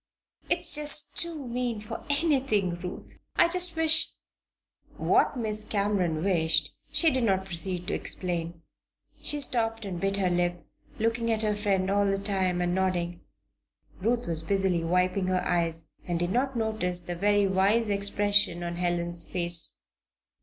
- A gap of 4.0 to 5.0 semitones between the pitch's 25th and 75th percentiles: Yes, average, 4.3 semitones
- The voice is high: Yes, high, 195 Hz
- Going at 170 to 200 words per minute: No, average, 155 wpm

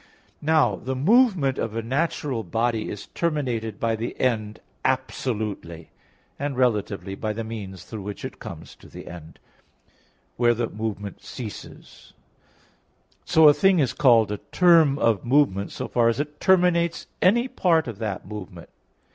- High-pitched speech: No, low, 120 Hz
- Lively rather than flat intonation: Yes, wide, 5.8 semitones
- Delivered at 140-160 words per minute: Yes, average, 150 wpm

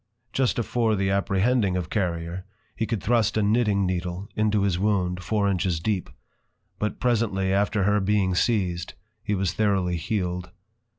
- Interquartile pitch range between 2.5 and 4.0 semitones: Yes, average, 2.9 semitones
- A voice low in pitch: Yes, low, 100 Hz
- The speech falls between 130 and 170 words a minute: Yes, average, 160 wpm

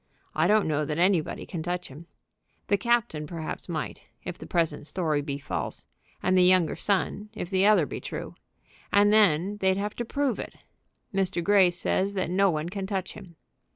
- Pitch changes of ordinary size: Yes, average, 3.5 semitones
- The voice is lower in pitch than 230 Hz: Yes, medium, 185 Hz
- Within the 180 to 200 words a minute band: Yes, average, 190 wpm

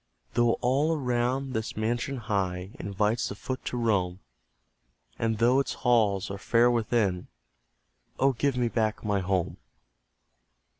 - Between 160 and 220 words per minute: No, slow, 135 wpm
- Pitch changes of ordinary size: Yes, average, 3.5 semitones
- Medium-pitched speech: No, low, 115 Hz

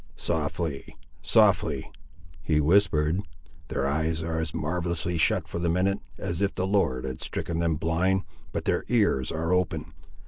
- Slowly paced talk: No, average, 150 wpm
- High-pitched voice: No, very low, 85 Hz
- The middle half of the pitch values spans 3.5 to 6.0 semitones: No, average, 2.7 semitones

